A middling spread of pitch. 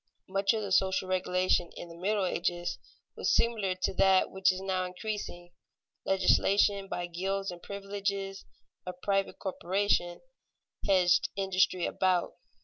No: narrow, 1.5 semitones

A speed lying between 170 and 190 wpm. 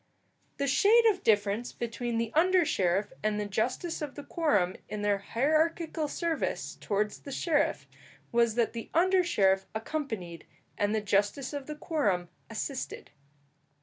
No: average, 150 wpm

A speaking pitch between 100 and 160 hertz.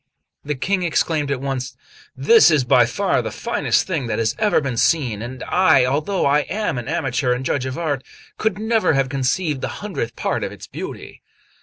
Yes: medium, 140 Hz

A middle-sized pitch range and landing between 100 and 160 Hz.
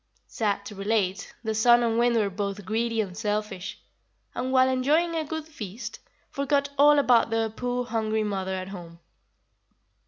No: average, 4.0 semitones; high, 225 Hz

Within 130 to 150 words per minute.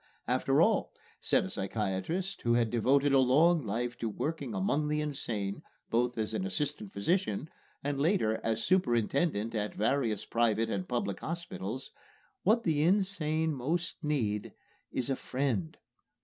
Yes: average, 145 wpm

